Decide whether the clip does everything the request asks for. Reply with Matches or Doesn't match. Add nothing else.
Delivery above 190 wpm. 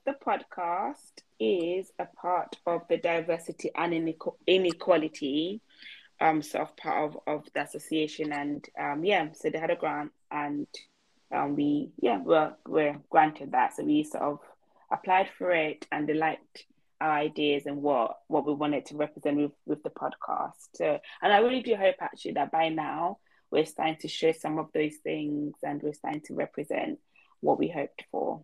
Doesn't match